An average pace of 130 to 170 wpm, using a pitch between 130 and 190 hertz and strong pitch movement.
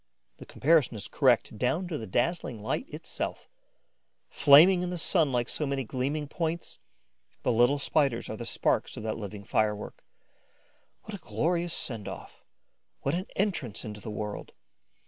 Yes: average, 160 wpm; low, 135 Hz; wide, 6.9 semitones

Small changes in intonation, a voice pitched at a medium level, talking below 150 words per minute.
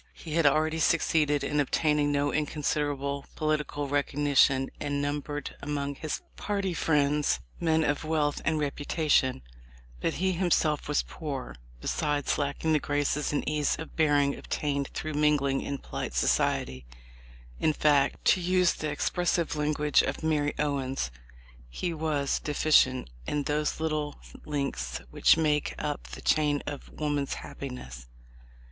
Yes: narrow, 1.5 semitones; medium, 145 Hz; average, 140 wpm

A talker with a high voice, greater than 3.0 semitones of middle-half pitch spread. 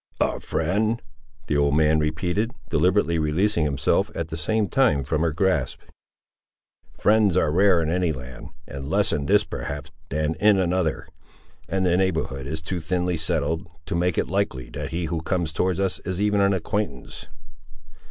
No: very low, 85 Hz; average, 3.8 semitones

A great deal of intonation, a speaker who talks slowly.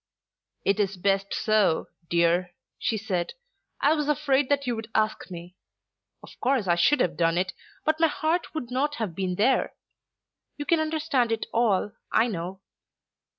No: wide, 7.5 semitones; average, 165 wpm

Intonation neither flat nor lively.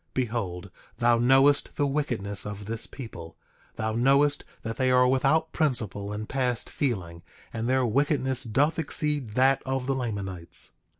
Yes: average, 4.2 semitones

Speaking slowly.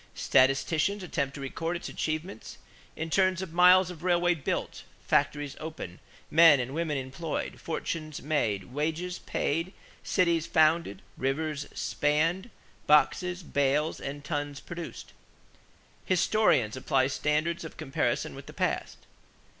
Yes: slow, 120 wpm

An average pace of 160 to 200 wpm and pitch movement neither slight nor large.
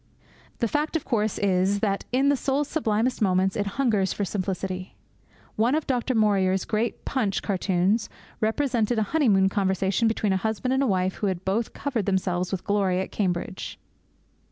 Yes: average, 165 wpm; average, 3.9 semitones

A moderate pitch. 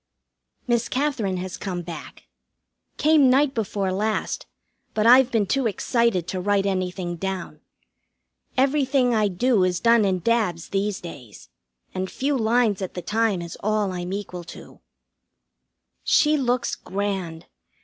No: high, 205 Hz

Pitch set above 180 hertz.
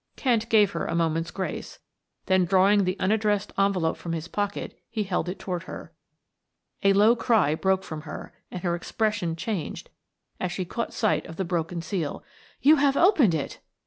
Yes: high, 190 Hz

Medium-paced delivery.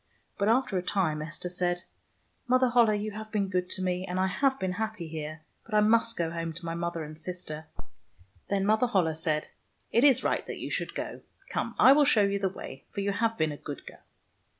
No: fast, 235 wpm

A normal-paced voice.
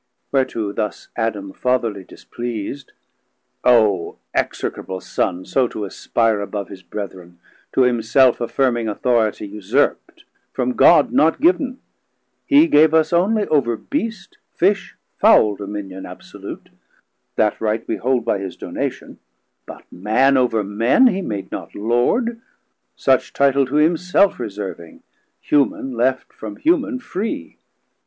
No: slow, 125 wpm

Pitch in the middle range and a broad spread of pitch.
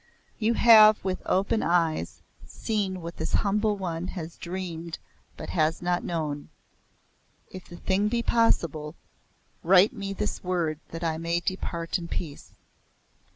No: medium, 180 Hz; average, 3.2 semitones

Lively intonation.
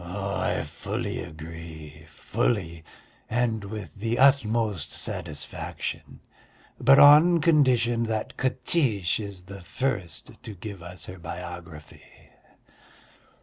Yes: wide, 5.9 semitones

